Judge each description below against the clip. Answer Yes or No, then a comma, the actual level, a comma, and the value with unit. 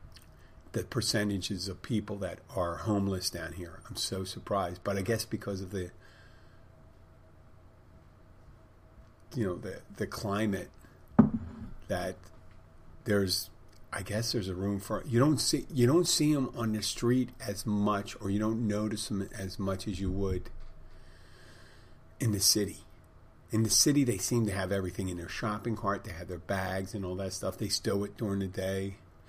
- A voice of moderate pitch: No, low, 100 Hz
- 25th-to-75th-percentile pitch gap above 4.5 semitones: No, average, 2.8 semitones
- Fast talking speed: No, average, 170 wpm